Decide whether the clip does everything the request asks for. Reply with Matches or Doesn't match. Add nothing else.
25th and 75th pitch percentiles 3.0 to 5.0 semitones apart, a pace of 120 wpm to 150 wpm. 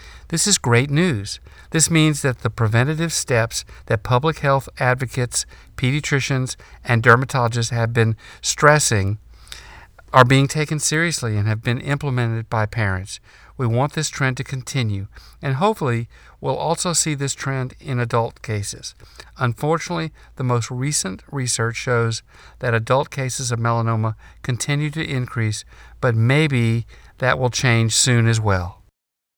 Matches